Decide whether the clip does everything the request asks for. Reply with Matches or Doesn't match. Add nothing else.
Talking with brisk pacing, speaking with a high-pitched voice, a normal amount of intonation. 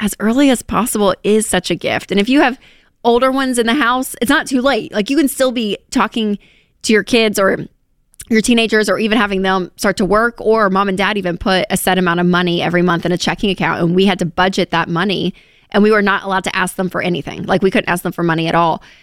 Matches